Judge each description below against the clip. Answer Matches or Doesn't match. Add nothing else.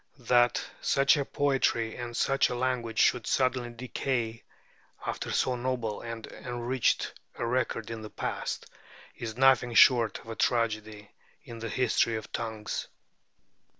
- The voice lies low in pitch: Matches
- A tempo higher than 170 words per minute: Doesn't match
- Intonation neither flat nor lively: Doesn't match